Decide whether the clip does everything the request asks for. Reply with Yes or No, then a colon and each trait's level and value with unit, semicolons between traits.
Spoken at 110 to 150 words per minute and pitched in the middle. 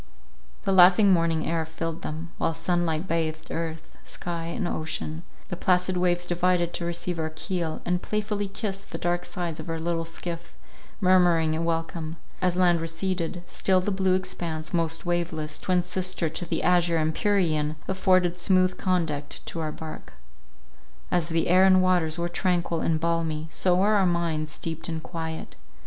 No: average, 165 wpm; medium, 170 Hz